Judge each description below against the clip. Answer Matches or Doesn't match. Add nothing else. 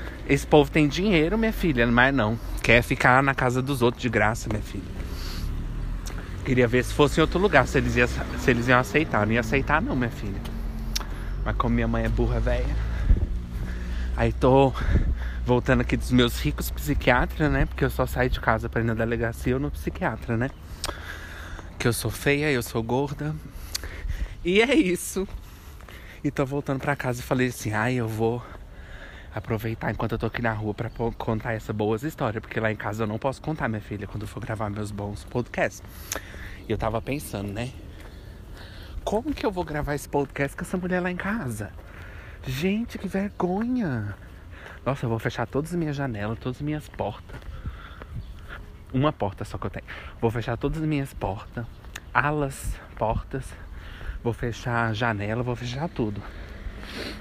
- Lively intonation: Matches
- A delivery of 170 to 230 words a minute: Matches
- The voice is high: Doesn't match